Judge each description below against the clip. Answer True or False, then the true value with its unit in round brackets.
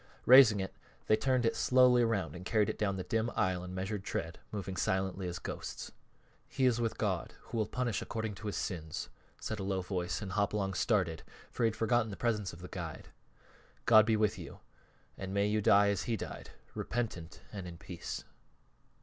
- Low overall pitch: True (100 Hz)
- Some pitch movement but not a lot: True (3.4 semitones)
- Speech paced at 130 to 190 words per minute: False (200 wpm)